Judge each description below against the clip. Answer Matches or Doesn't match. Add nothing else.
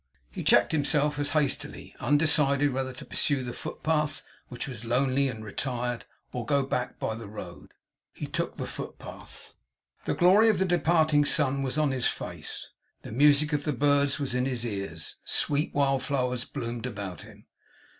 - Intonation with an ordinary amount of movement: Matches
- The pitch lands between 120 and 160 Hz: Matches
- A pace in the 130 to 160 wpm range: Doesn't match